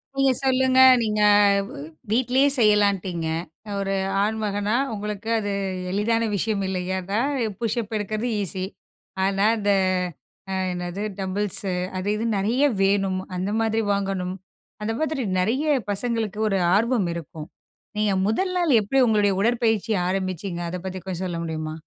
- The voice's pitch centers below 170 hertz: No, high, 205 Hz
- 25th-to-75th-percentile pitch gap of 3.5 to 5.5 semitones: No, average, 3.1 semitones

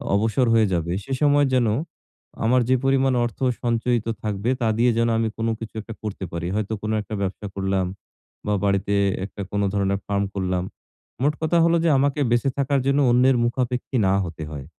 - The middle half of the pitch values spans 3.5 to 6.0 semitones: Yes, average, 4.6 semitones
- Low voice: Yes, low, 115 Hz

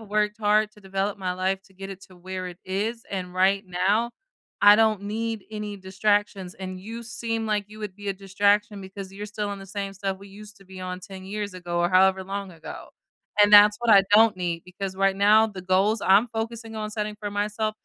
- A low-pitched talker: No, high, 200 Hz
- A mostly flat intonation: Yes, narrow, 1.9 semitones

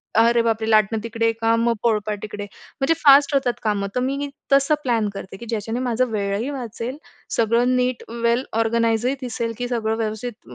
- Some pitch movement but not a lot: No, narrow, 2.2 semitones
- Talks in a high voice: Yes, high, 230 Hz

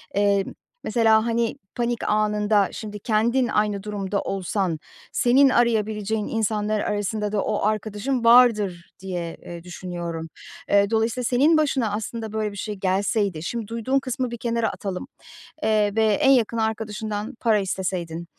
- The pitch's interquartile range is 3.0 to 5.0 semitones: No, narrow, 2.5 semitones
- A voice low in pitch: No, high, 215 Hz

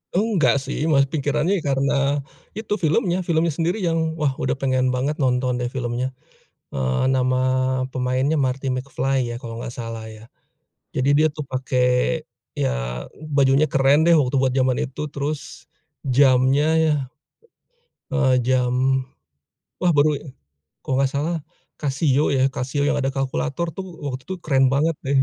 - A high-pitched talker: No, low, 135 Hz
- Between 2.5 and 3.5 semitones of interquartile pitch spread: Yes, average, 2.9 semitones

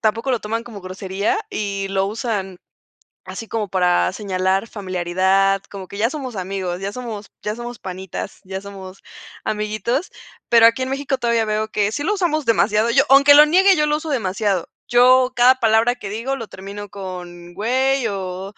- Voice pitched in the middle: No, high, 215 Hz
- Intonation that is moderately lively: Yes, average, 4.2 semitones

